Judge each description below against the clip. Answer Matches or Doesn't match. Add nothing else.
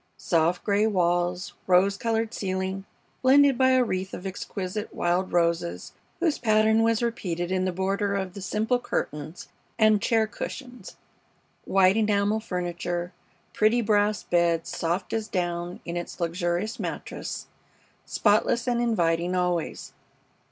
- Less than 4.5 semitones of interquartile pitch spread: Matches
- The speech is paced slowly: Matches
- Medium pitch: Doesn't match